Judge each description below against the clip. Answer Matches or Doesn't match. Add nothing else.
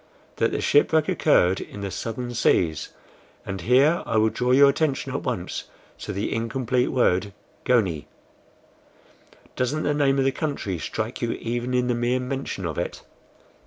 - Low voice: Matches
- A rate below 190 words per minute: Matches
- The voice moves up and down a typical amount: Matches